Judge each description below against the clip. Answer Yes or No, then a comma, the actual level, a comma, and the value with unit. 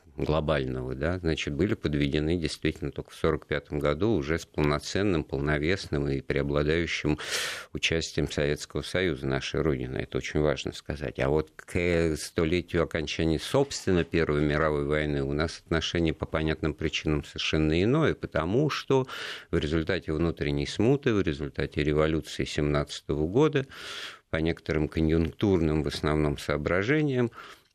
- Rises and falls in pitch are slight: Yes, narrow, 2.2 semitones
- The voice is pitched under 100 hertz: Yes, very low, 80 Hz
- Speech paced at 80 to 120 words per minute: No, average, 130 wpm